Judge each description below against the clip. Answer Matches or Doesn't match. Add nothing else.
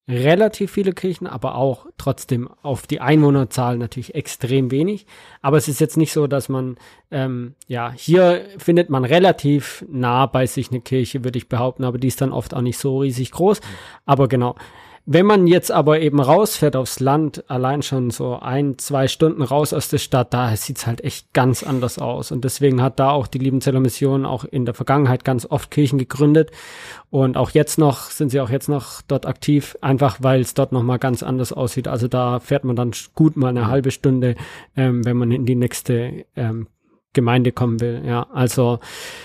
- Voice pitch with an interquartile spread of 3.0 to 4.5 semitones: Doesn't match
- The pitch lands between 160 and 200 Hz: Doesn't match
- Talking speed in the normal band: Doesn't match